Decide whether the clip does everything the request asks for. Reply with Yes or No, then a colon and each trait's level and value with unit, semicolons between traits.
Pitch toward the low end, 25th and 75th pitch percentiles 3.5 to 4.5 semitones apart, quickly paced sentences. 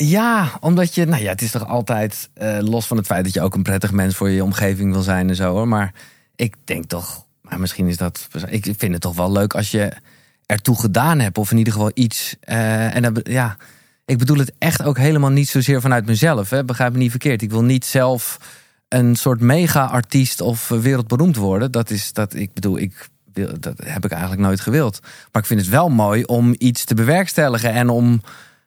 Yes: low, 115 Hz; average, 4.0 semitones; fast, 225 wpm